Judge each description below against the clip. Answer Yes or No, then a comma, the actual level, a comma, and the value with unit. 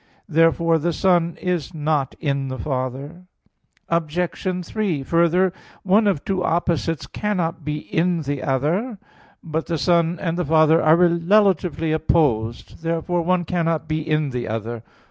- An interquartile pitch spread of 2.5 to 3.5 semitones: Yes, average, 2.9 semitones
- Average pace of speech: Yes, average, 145 wpm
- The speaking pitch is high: No, medium, 165 Hz